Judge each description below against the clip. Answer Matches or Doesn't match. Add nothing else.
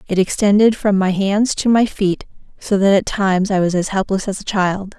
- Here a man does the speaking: Doesn't match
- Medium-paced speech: Doesn't match